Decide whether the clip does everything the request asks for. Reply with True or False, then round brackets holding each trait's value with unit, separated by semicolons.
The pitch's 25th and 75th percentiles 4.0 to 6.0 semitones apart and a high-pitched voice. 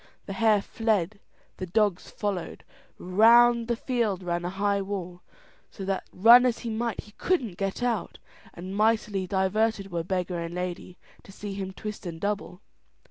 False (3.4 semitones; 200 Hz)